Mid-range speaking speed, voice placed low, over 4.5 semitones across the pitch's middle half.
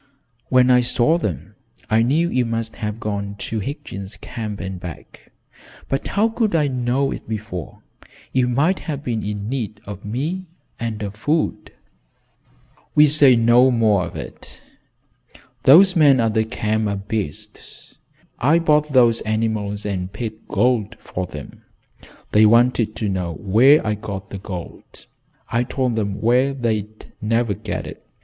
No: average, 155 wpm; low, 115 Hz; average, 3.9 semitones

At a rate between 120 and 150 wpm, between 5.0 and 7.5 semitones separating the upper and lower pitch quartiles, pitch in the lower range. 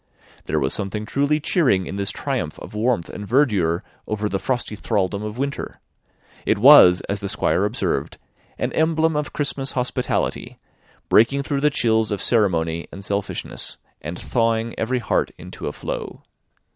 No: average, 160 wpm; wide, 5.5 semitones; low, 110 Hz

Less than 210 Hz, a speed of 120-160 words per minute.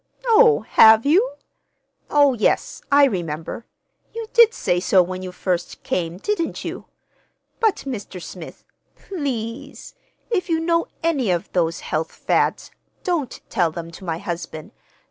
No: high, 220 Hz; average, 140 wpm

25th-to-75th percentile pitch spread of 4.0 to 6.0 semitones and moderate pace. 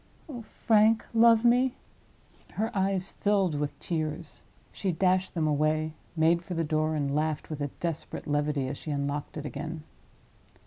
Yes: average, 4.6 semitones; average, 160 wpm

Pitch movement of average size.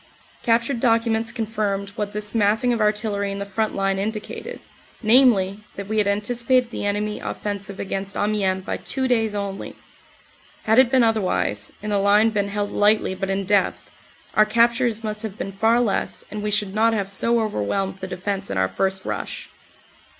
No: narrow, 2.2 semitones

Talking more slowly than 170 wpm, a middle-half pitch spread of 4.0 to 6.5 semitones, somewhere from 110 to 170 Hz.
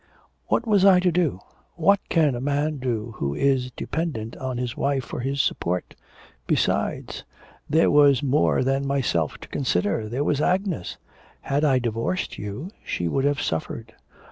Yes: average, 160 wpm; average, 4.5 semitones; low, 135 Hz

